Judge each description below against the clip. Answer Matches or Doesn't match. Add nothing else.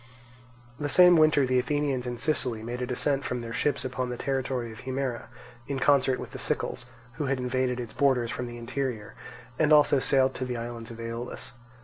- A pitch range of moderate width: Doesn't match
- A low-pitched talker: Matches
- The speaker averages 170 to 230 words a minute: Matches